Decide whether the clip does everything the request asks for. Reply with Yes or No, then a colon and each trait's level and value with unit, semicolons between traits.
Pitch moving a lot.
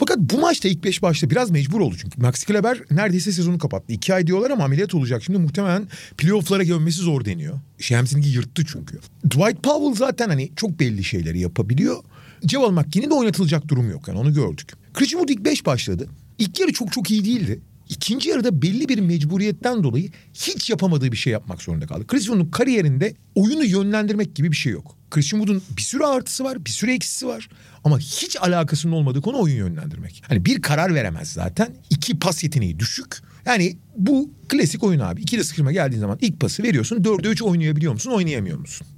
Yes: wide, 7.0 semitones